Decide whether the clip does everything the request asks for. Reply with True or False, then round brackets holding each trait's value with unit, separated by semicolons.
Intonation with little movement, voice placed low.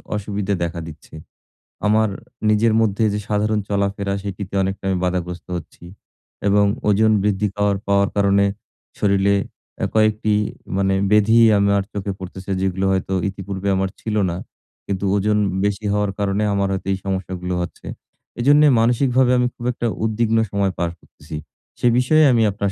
True (1.8 semitones; 100 Hz)